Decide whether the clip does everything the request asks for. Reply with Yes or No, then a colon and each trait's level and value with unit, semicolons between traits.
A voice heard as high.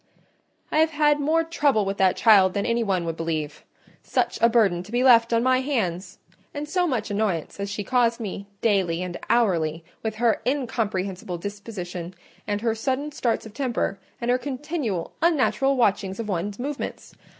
Yes: high, 220 Hz